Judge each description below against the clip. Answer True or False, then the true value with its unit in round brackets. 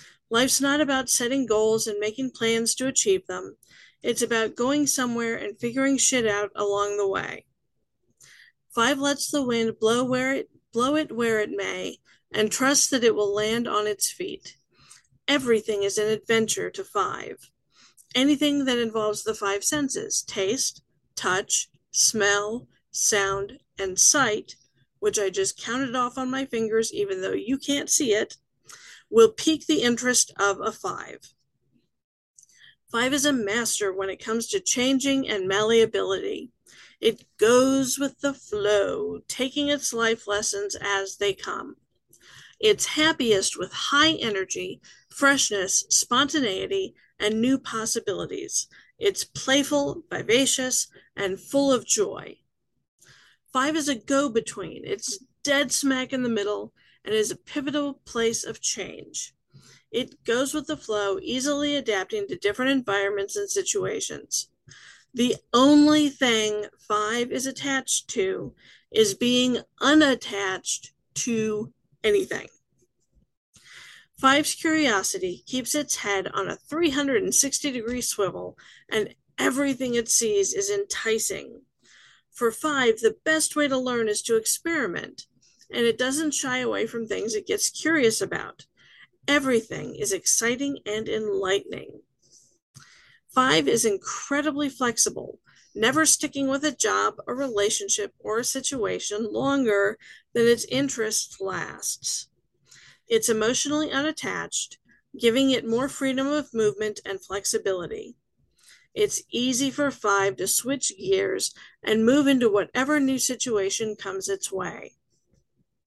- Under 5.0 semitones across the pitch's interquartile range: False (5.4 semitones)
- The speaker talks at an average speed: False (130 wpm)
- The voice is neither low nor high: False (260 Hz)